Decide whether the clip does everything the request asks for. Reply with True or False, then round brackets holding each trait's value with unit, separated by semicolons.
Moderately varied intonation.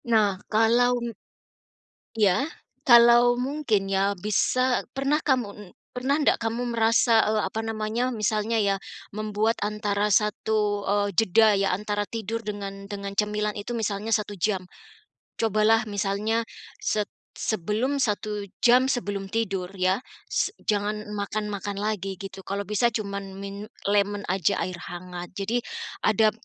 False (2.0 semitones)